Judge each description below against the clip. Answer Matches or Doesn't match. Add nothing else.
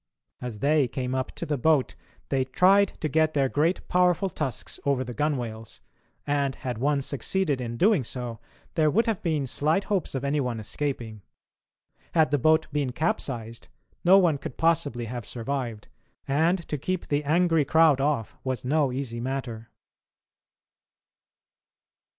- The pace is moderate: Matches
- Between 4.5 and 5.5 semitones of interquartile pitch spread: Doesn't match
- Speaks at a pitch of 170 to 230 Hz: Doesn't match